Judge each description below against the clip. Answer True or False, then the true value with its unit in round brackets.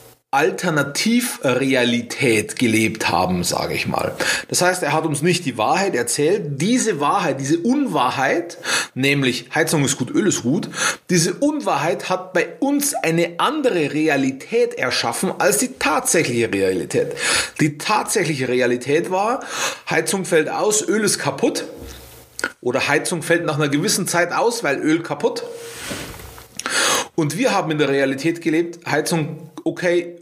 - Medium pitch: True (160 Hz)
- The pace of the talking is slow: False (135 wpm)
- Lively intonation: True (5.9 semitones)